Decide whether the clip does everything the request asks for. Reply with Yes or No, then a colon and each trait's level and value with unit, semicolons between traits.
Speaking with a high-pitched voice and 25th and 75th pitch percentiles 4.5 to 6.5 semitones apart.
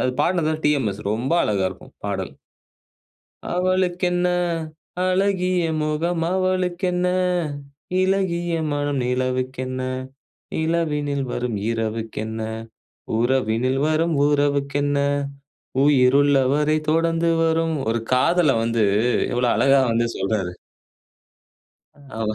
No: medium, 145 Hz; average, 5.3 semitones